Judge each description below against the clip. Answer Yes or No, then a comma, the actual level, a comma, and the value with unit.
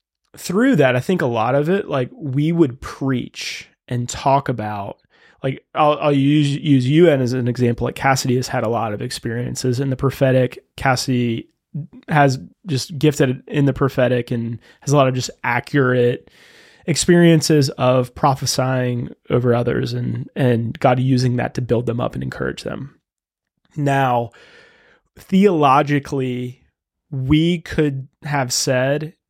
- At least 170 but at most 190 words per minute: No, average, 145 wpm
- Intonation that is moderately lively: Yes, average, 3.2 semitones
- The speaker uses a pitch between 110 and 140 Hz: Yes, low, 135 Hz